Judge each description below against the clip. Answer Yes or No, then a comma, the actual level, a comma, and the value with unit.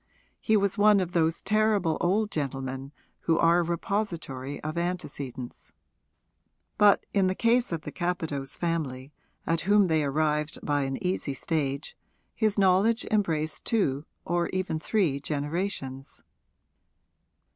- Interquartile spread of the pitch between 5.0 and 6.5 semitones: Yes, average, 5.3 semitones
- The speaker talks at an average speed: No, slow, 130 wpm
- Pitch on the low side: No, medium, 165 Hz